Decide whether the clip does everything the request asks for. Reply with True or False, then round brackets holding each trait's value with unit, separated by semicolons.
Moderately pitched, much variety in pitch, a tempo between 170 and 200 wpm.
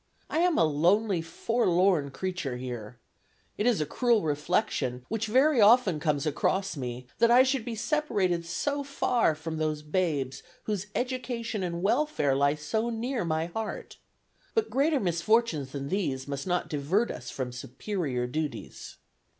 False (180 Hz; 8.0 semitones; 150 wpm)